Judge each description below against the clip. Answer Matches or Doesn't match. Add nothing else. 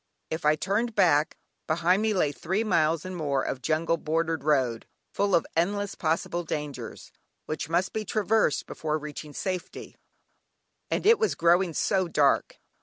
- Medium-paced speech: Matches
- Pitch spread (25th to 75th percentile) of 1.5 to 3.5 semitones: Doesn't match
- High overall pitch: Doesn't match